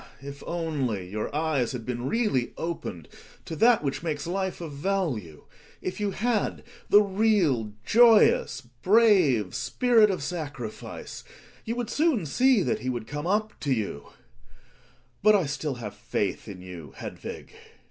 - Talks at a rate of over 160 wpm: No, average, 150 wpm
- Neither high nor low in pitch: Yes, medium, 155 Hz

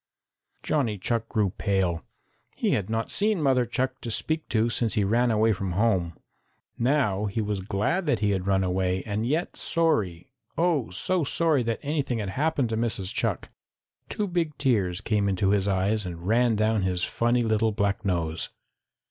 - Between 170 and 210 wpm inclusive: Yes, average, 175 wpm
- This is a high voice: No, low, 110 Hz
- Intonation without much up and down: No, average, 4.8 semitones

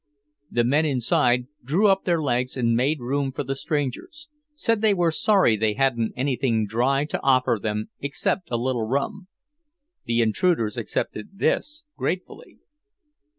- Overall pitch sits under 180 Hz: Yes, low, 135 Hz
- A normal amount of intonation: No, wide, 6.1 semitones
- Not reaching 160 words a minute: Yes, average, 150 wpm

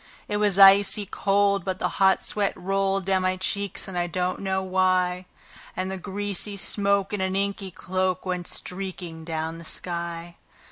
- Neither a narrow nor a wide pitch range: No, narrow, 1.5 semitones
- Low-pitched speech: No, high, 190 Hz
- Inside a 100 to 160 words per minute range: No, average, 170 wpm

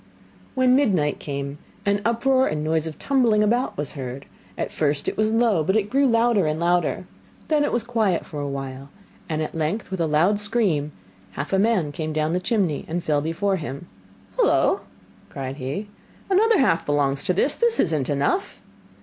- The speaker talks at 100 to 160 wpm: No, average, 190 wpm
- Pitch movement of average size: No, wide, 7.4 semitones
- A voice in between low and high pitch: Yes, medium, 175 Hz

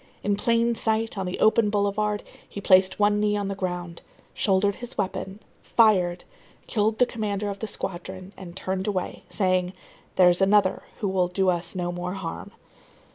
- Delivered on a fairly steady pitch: Yes, narrow, 2.2 semitones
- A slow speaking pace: No, average, 170 wpm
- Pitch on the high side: Yes, high, 195 Hz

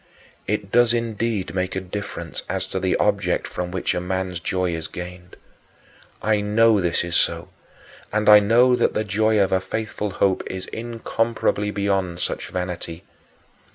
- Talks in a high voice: No, low, 100 Hz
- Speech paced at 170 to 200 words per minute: No, average, 160 wpm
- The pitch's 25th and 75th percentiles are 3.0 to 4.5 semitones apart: Yes, average, 3.3 semitones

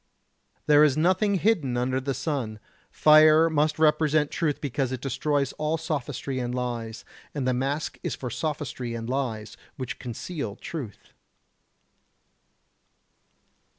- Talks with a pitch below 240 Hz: Yes, medium, 140 Hz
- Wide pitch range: No, average, 3.6 semitones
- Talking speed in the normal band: No, slow, 125 wpm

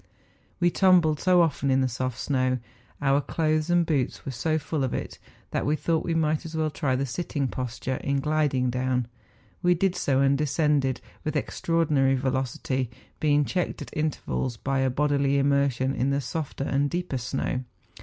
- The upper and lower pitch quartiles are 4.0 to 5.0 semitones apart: No, average, 3.0 semitones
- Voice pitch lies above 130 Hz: Yes, medium, 140 Hz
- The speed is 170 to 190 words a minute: Yes, average, 180 wpm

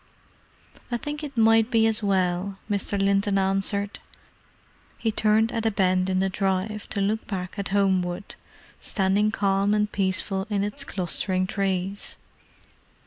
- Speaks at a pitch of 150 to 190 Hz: No, high, 200 Hz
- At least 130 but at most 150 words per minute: Yes, average, 140 wpm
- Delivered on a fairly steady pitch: Yes, narrow, 1.9 semitones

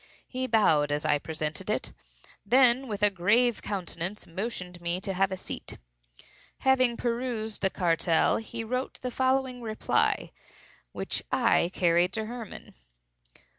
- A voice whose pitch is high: Yes, high, 215 Hz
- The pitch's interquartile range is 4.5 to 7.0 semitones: Yes, wide, 5.4 semitones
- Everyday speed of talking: No, slow, 130 wpm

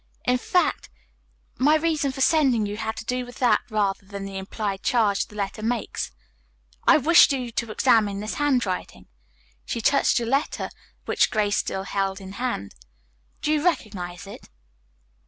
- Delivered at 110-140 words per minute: No, average, 165 wpm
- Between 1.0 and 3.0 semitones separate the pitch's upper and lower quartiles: No, average, 4.7 semitones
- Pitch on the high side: Yes, high, 225 Hz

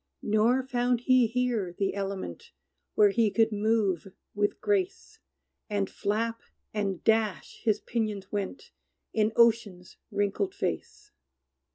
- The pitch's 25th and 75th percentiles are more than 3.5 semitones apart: No, average, 2.9 semitones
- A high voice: Yes, high, 215 Hz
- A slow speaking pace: Yes, slow, 115 wpm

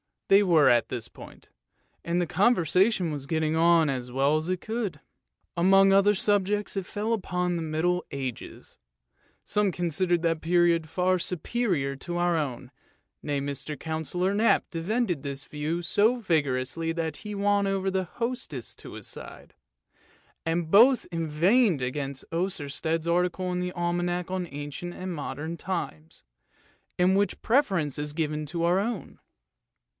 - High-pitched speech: No, medium, 175 Hz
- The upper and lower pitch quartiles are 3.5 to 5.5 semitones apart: Yes, average, 3.8 semitones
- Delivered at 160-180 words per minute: No, average, 150 wpm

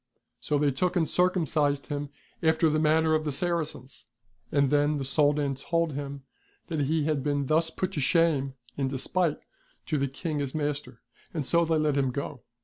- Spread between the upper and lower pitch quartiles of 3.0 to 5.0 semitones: No, narrow, 2.4 semitones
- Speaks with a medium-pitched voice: Yes, medium, 150 Hz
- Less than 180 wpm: No, average, 185 wpm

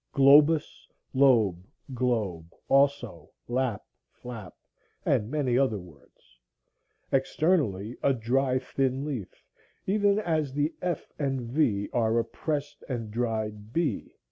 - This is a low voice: Yes, low, 130 Hz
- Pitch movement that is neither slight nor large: Yes, average, 4.8 semitones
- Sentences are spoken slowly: Yes, slow, 115 wpm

